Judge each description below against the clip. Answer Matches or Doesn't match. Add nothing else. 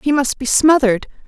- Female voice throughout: Matches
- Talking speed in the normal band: Matches